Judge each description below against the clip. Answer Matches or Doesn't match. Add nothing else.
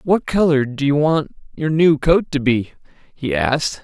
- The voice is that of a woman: Doesn't match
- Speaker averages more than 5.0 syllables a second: Doesn't match